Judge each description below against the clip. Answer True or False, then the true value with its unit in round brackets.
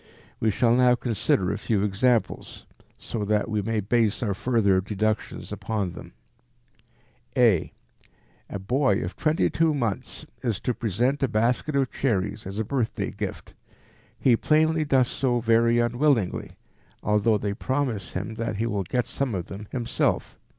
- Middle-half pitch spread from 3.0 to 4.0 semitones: True (3.5 semitones)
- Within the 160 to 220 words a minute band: False (150 wpm)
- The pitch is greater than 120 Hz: False (115 Hz)